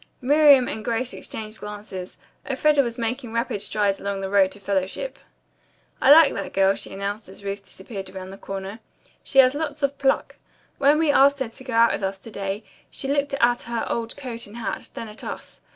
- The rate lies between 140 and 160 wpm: No, fast, 205 wpm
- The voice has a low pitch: No, high, 230 Hz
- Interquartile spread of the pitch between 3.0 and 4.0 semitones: No, average, 5.3 semitones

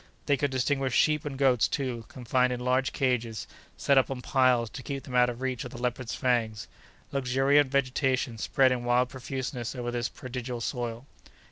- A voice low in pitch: Yes, low, 125 Hz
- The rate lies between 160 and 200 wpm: Yes, average, 180 wpm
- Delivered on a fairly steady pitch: Yes, narrow, 1.7 semitones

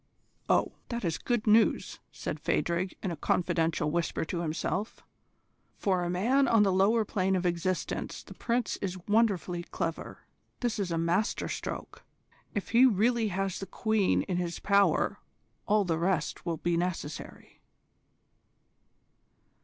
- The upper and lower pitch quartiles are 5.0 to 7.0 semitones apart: No, average, 3.8 semitones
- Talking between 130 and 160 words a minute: Yes, average, 145 wpm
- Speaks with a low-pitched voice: No, medium, 185 Hz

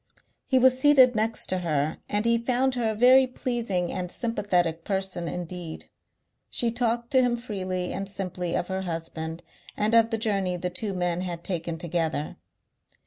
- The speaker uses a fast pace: No, average, 170 wpm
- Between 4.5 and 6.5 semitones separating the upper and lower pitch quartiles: Yes, average, 4.9 semitones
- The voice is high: Yes, high, 195 Hz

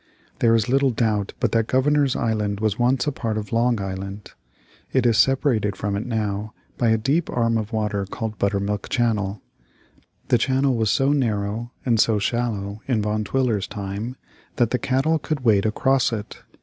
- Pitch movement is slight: No, average, 3.3 semitones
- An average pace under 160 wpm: No, average, 175 wpm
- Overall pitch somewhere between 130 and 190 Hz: No, low, 110 Hz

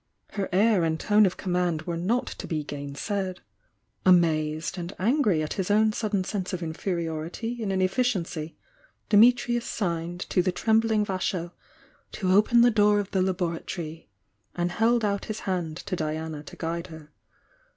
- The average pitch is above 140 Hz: Yes, medium, 185 Hz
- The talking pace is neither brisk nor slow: Yes, average, 160 wpm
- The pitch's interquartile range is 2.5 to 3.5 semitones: No, average, 4.1 semitones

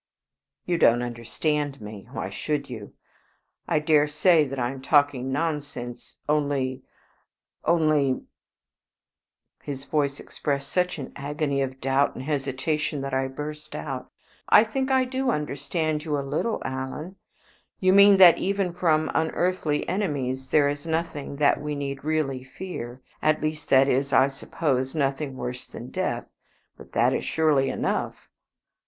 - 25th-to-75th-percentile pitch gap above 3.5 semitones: No, average, 2.9 semitones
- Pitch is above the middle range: No, medium, 145 Hz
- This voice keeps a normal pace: Yes, average, 150 wpm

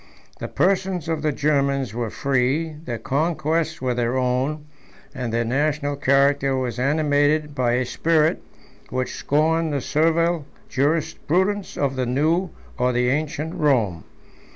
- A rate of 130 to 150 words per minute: Yes, slow, 135 wpm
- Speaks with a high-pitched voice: No, medium, 145 Hz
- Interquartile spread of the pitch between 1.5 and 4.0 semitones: Yes, average, 3.6 semitones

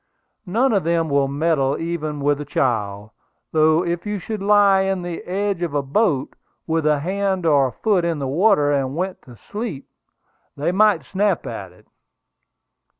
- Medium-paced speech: Yes, average, 170 wpm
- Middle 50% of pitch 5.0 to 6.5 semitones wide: Yes, wide, 5.4 semitones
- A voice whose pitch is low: No, medium, 165 Hz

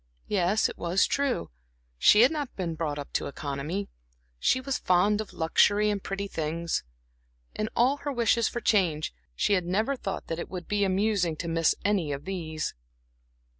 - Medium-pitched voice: No, high, 195 Hz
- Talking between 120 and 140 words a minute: No, average, 175 wpm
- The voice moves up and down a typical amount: Yes, average, 4.5 semitones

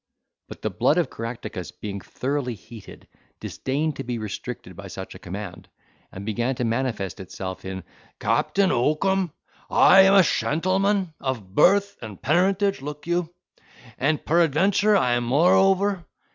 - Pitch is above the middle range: No, medium, 145 Hz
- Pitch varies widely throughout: Yes, wide, 8.6 semitones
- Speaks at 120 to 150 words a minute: Yes, average, 145 wpm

